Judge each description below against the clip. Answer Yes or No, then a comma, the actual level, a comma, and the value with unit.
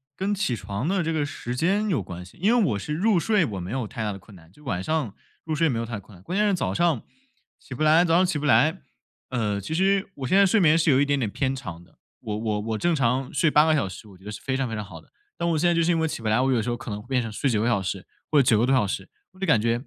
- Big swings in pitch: Yes, wide, 7.4 semitones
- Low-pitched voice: Yes, low, 130 Hz